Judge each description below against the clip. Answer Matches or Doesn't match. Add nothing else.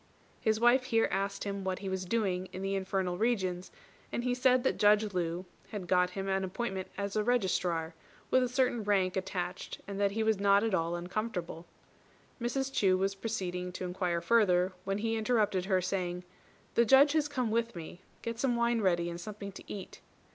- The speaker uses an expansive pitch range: Doesn't match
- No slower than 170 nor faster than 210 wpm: Matches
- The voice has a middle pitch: Doesn't match